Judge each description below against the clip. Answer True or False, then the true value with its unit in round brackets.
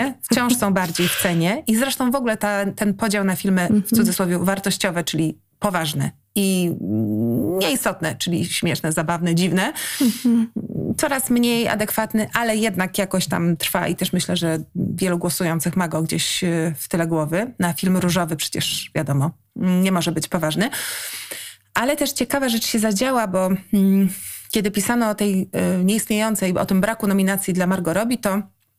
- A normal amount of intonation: True (4.2 semitones)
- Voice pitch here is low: False (190 Hz)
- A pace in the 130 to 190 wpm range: True (155 wpm)